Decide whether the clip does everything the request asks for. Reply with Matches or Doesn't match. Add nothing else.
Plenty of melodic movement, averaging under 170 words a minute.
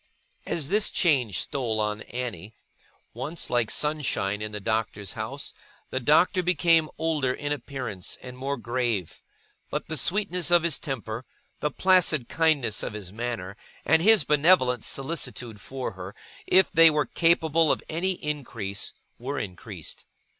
Matches